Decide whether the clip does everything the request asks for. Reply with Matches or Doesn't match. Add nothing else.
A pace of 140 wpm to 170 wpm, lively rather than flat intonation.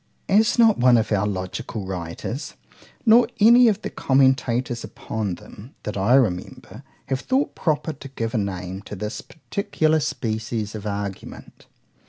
Matches